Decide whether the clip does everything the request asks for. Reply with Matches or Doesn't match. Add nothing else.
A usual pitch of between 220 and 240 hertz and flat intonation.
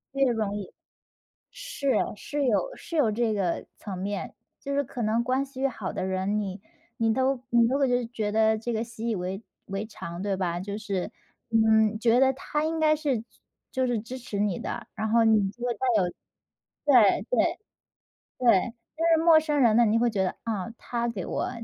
Doesn't match